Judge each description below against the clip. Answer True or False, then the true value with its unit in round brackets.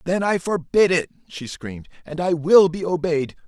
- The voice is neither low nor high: True (170 Hz)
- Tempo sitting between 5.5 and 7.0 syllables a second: False (4.8 syllables/s)